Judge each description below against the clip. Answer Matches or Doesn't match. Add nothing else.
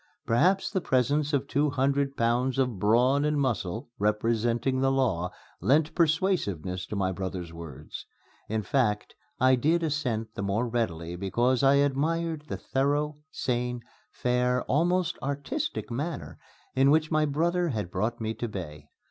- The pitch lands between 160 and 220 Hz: Doesn't match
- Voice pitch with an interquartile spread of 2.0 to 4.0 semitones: Doesn't match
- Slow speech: Doesn't match